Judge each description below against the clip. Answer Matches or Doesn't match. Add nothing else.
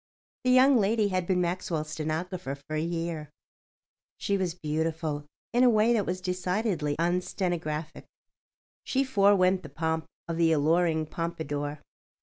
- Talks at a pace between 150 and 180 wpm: Doesn't match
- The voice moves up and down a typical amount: Matches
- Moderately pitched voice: Matches